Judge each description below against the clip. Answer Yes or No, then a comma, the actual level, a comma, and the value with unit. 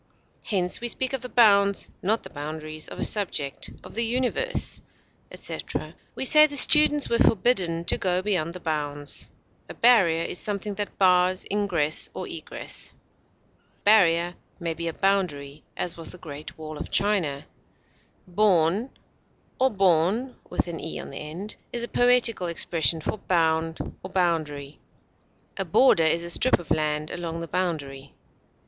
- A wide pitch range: No, average, 4.8 semitones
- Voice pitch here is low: No, medium, 180 Hz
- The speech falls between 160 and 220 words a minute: No, average, 145 wpm